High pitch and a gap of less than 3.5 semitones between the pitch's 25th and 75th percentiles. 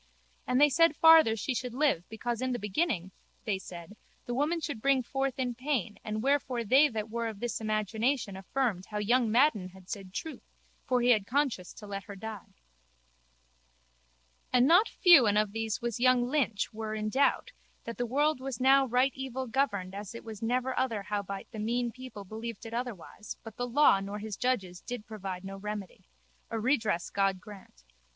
No: high, 230 Hz; average, 3.9 semitones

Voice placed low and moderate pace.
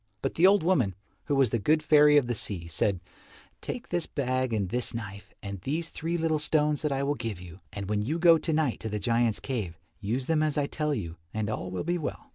No: low, 130 Hz; fast, 245 wpm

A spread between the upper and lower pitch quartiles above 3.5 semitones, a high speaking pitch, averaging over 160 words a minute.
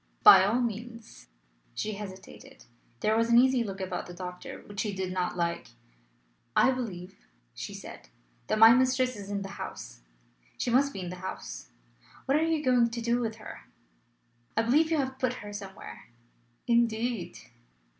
Yes: average, 4.5 semitones; high, 225 Hz; average, 170 wpm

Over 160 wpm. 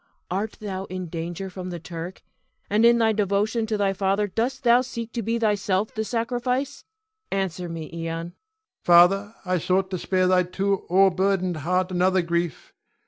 Yes: average, 170 wpm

